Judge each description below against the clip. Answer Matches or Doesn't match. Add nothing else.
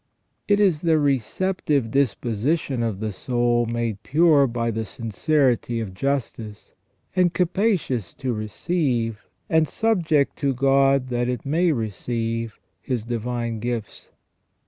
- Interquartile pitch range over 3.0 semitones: Matches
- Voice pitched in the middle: Doesn't match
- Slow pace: Matches